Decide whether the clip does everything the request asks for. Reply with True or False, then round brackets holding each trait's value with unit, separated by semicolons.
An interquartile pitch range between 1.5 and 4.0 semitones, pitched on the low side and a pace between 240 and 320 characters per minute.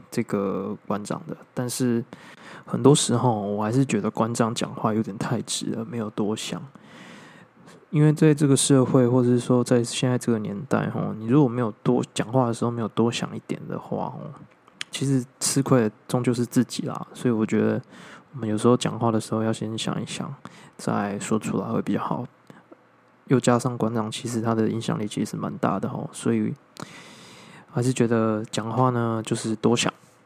True (2.5 semitones; 120 Hz; 275 characters per minute)